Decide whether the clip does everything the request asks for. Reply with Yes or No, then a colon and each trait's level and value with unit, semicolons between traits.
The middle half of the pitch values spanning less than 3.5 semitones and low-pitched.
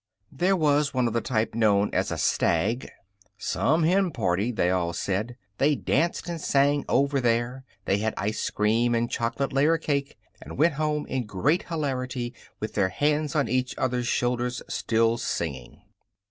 No: average, 4.7 semitones; low, 125 Hz